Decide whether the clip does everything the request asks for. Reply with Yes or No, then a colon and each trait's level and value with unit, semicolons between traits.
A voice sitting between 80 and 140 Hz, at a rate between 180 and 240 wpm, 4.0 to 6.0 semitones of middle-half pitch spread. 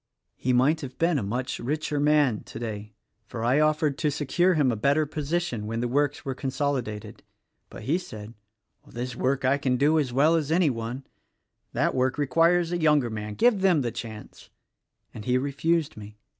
Yes: low, 135 Hz; average, 190 wpm; average, 4.3 semitones